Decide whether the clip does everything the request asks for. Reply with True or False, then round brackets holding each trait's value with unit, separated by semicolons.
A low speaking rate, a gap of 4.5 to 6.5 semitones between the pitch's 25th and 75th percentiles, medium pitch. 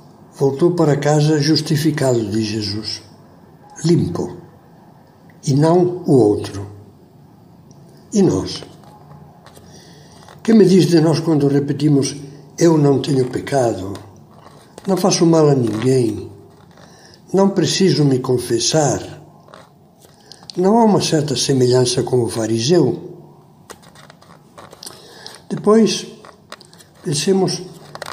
True (90 wpm; 5.3 semitones; 155 Hz)